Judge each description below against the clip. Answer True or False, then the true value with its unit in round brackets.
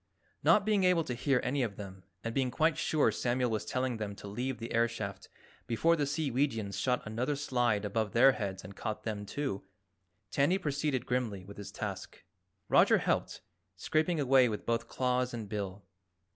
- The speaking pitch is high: False (120 Hz)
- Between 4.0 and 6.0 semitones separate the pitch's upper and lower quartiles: True (4.8 semitones)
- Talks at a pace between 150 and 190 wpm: True (180 wpm)